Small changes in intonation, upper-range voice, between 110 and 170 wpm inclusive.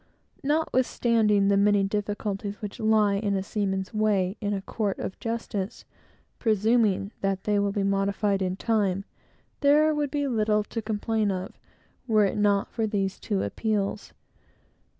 Yes: narrow, 2.0 semitones; high, 205 Hz; average, 150 wpm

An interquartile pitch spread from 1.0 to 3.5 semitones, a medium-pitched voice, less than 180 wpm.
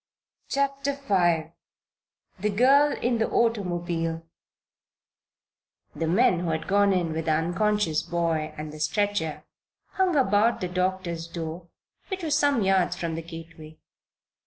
No: average, 5.2 semitones; medium, 180 Hz; slow, 135 wpm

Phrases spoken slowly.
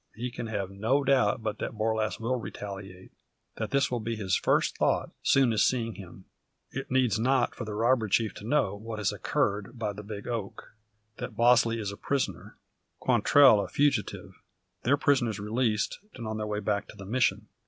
No: average, 190 wpm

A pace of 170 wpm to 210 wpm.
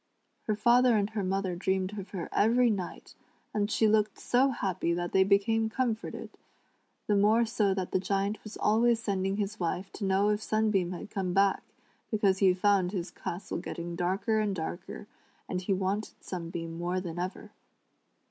Yes: average, 175 wpm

